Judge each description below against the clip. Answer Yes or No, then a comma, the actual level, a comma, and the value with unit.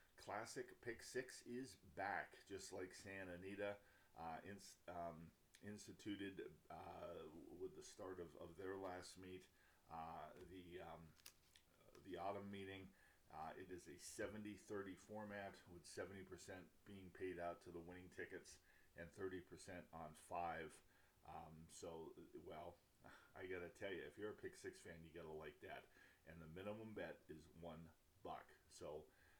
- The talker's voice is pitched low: Yes, very low, 95 Hz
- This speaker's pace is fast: No, average, 145 wpm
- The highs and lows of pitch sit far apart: No, average, 3.2 semitones